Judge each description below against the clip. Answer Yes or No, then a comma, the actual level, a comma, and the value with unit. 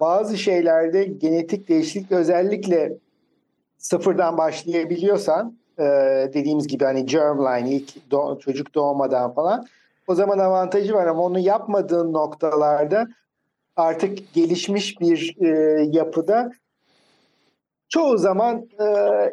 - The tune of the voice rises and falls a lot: No, average, 4.8 semitones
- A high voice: No, medium, 175 Hz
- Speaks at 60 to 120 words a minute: Yes, average, 100 wpm